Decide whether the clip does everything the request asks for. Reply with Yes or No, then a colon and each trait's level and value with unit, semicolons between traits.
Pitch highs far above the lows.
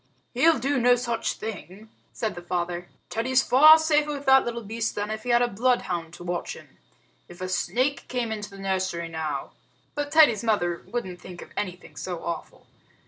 Yes: wide, 5.8 semitones